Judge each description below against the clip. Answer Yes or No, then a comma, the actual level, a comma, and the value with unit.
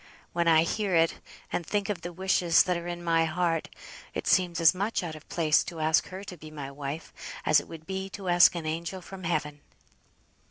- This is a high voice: No, medium, 170 Hz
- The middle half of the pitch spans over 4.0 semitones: No, narrow, 2.5 semitones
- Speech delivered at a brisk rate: Yes, fast, 215 wpm